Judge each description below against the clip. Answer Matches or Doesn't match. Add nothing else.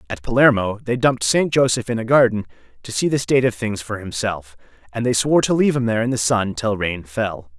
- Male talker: Matches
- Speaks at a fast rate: Matches